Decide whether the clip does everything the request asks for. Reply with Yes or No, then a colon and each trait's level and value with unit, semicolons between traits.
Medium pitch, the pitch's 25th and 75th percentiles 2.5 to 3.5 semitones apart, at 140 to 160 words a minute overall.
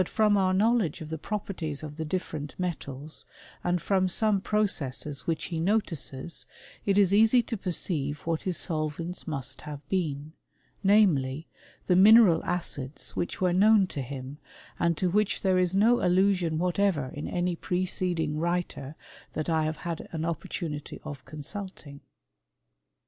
No: medium, 175 Hz; average, 4.1 semitones; average, 150 wpm